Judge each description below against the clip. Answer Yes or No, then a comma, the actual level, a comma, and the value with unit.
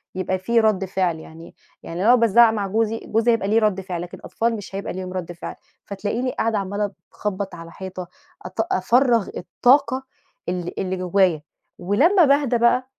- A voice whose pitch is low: No, high, 200 Hz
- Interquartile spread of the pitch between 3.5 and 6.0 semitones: Yes, average, 3.8 semitones